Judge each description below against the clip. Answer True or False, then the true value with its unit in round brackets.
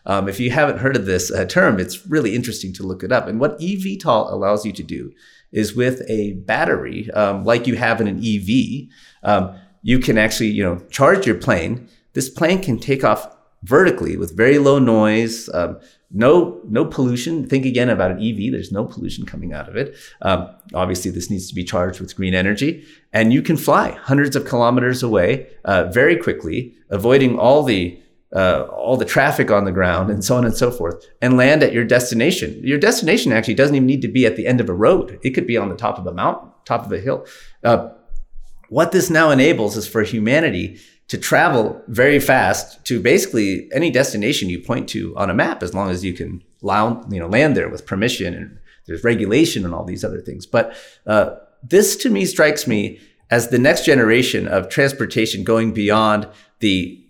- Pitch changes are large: False (4.2 semitones)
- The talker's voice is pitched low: True (115 Hz)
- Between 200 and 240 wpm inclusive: True (205 wpm)